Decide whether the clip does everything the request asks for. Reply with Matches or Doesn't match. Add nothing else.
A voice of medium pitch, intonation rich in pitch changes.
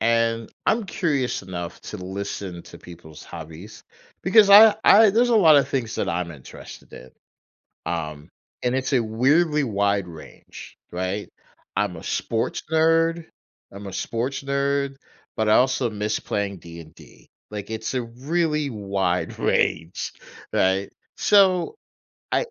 Doesn't match